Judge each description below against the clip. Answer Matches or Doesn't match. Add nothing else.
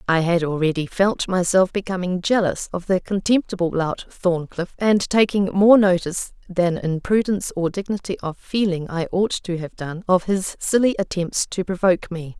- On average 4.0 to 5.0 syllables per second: Matches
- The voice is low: Doesn't match